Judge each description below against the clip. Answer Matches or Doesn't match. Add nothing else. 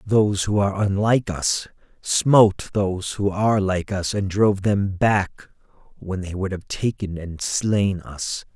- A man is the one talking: Matches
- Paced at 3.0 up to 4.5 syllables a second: Matches